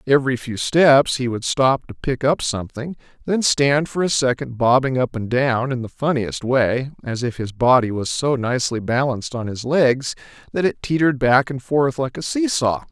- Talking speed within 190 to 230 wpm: Yes, average, 200 wpm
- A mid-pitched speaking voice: No, low, 130 Hz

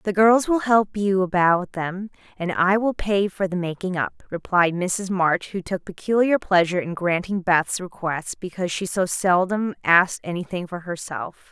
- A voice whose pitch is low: No, medium, 185 Hz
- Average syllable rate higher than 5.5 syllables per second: No, 4.7 syllables/s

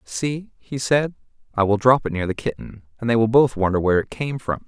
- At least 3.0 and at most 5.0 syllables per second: No, 5.5 syllables/s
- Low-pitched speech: Yes, low, 115 Hz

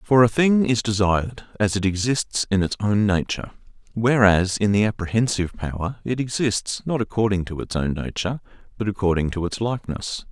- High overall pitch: No, low, 105 Hz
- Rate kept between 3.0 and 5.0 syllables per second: No, 5.5 syllables/s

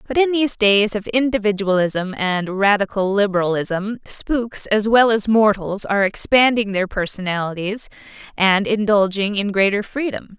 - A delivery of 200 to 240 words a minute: No, slow, 135 wpm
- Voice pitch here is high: Yes, high, 205 Hz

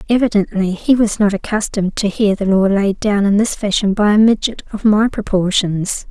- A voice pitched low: No, high, 205 Hz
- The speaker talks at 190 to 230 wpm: Yes, average, 195 wpm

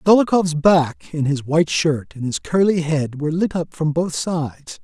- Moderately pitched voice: Yes, medium, 160 Hz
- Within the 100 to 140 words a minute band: No, average, 200 wpm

